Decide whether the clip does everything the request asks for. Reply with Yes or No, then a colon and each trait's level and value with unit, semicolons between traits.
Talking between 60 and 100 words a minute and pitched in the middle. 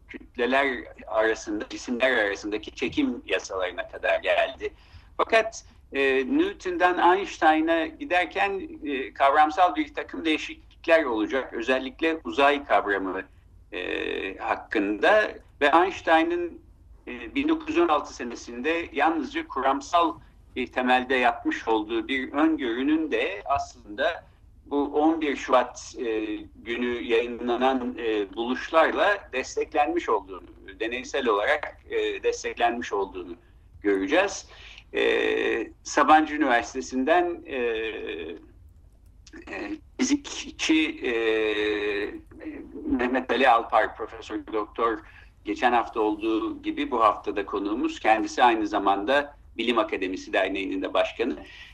No: slow, 95 wpm; very high, 285 Hz